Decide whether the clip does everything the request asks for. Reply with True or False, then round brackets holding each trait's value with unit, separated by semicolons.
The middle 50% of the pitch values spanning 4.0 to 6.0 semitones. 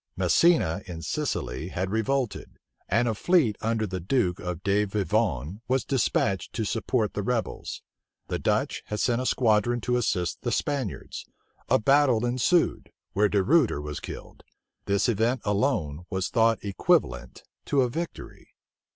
True (4.4 semitones)